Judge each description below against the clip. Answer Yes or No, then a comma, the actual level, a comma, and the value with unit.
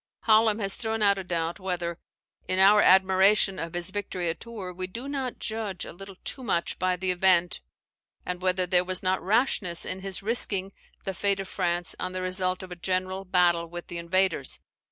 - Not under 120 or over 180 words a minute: No, average, 195 wpm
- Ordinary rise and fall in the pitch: No, narrow, 1.8 semitones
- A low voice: No, medium, 185 Hz